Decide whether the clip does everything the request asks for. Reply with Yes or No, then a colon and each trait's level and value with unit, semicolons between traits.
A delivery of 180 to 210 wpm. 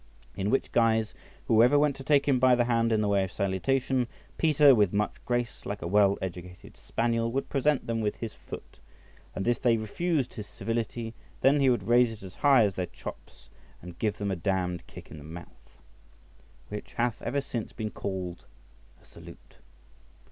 Yes: average, 190 wpm